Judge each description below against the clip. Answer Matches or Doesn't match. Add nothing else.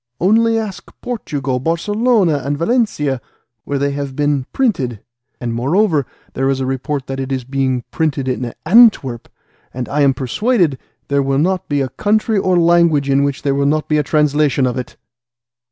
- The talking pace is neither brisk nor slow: Matches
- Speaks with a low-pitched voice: Doesn't match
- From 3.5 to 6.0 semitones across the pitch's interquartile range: Matches